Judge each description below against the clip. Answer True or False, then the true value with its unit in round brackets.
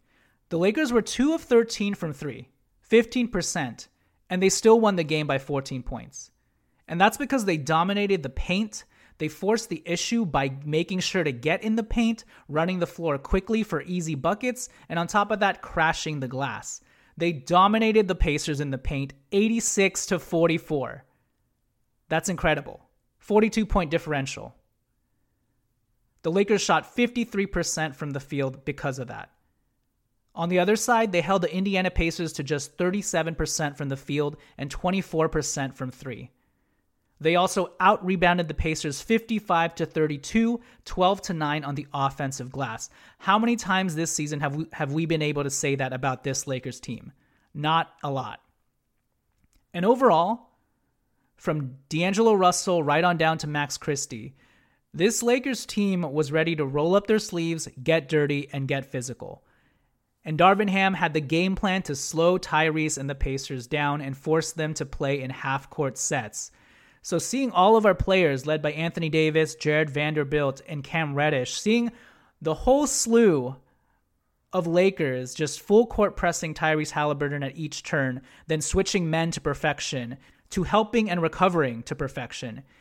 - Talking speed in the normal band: True (160 wpm)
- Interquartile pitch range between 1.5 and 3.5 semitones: False (4.7 semitones)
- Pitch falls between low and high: True (160 Hz)